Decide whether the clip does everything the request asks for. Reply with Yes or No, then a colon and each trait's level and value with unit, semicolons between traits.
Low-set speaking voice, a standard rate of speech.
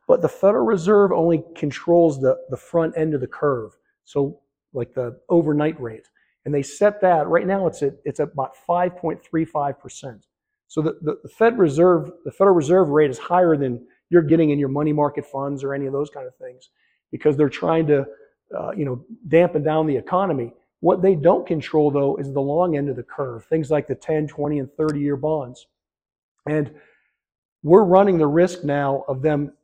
No: medium, 150 Hz; average, 195 wpm